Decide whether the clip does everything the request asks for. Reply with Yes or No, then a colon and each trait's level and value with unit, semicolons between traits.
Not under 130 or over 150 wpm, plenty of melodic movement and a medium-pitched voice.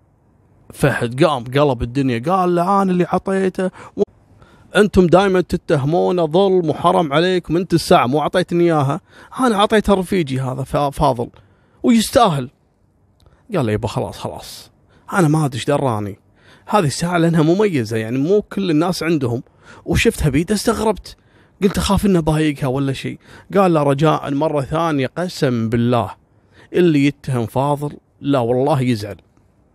Yes: fast, 135 wpm; wide, 6.2 semitones; medium, 150 Hz